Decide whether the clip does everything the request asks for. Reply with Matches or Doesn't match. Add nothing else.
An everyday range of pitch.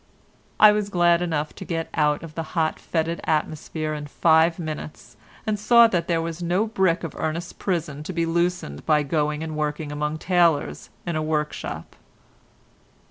Doesn't match